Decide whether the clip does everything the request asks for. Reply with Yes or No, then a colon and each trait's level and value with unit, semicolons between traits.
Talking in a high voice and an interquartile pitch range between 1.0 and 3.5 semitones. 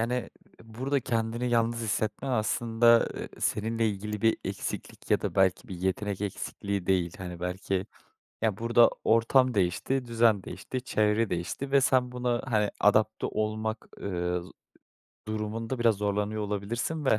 No: low, 110 Hz; average, 2.7 semitones